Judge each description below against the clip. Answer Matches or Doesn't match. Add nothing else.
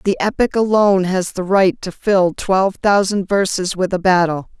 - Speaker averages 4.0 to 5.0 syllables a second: Matches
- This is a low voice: Doesn't match